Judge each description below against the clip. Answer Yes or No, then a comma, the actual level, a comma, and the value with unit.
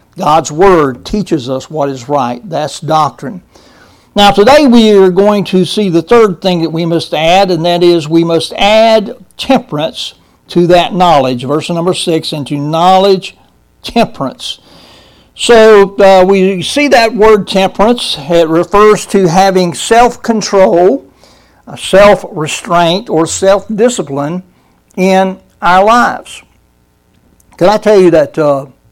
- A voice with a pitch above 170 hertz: Yes, medium, 185 Hz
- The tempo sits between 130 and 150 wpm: Yes, slow, 135 wpm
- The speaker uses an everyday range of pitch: Yes, average, 4.1 semitones